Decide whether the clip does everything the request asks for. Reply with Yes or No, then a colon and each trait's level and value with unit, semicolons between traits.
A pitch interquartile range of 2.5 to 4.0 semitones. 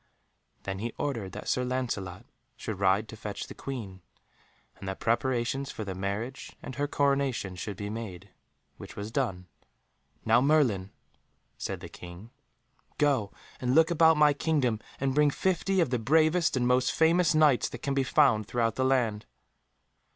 No: wide, 5.4 semitones